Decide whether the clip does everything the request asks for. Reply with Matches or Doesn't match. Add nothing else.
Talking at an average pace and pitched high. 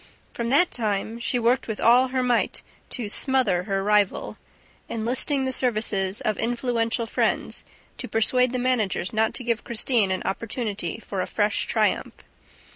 Matches